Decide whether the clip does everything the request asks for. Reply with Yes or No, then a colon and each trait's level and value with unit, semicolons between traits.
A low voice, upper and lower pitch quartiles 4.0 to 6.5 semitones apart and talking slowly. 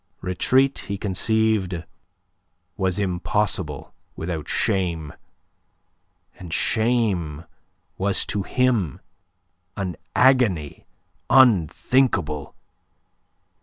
Yes: very low, 95 Hz; average, 4.5 semitones; slow, 65 wpm